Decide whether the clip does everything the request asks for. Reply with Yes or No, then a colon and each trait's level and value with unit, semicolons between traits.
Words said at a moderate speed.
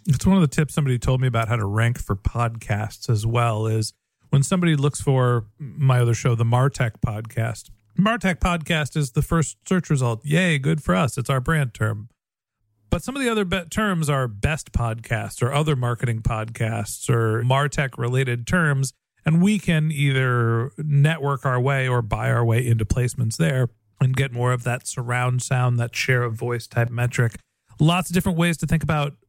Yes: average, 195 wpm